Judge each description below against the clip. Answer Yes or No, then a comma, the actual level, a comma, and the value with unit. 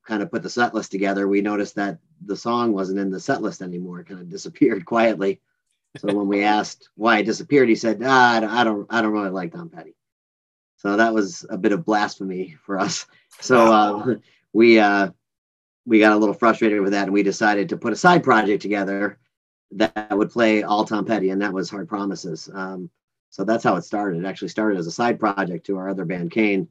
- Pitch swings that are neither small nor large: No, narrow, 2.3 semitones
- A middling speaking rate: No, fast, 225 wpm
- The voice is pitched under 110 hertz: Yes, low, 100 Hz